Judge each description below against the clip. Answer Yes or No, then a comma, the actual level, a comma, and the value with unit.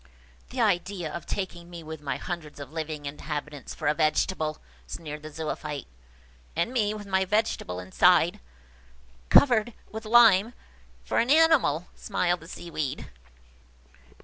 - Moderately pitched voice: Yes, medium, 170 Hz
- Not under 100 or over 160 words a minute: Yes, average, 140 wpm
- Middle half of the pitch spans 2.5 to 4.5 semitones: No, wide, 5.5 semitones